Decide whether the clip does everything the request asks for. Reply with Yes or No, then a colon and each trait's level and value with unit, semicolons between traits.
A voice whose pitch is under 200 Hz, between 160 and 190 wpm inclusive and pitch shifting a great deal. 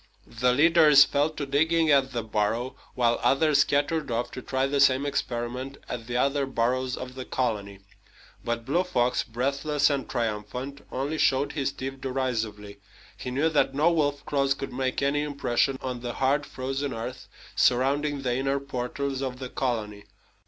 No: low, 135 Hz; average, 165 wpm; narrow, 2.4 semitones